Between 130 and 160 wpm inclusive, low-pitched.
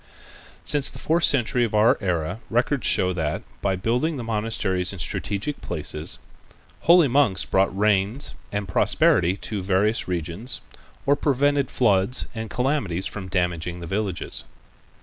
Yes: average, 145 wpm; low, 105 Hz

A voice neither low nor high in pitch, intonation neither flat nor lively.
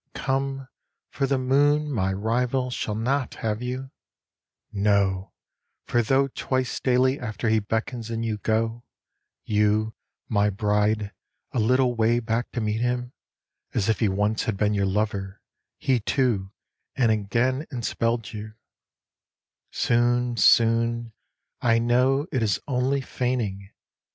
No: low, 115 Hz; average, 3.1 semitones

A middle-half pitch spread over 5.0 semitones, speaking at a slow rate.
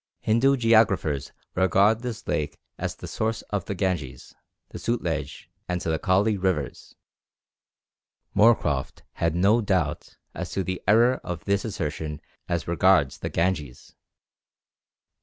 Yes: wide, 5.4 semitones; slow, 125 wpm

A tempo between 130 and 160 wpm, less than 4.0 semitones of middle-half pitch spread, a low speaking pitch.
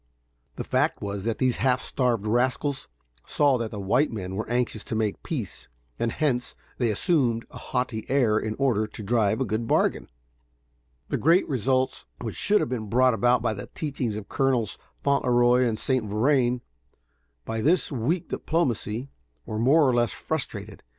No: average, 170 wpm; average, 3.4 semitones; low, 120 Hz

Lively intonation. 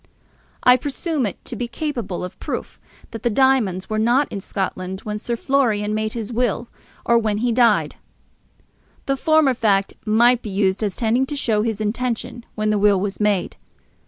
No: average, 3.1 semitones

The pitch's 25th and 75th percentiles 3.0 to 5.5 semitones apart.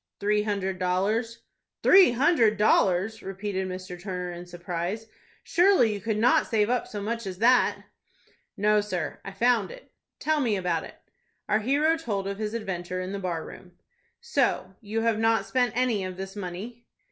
Yes: average, 3.8 semitones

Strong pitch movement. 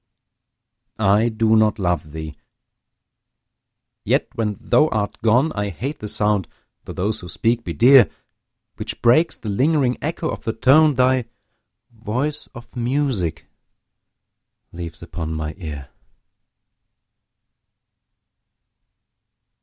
Yes: wide, 6.2 semitones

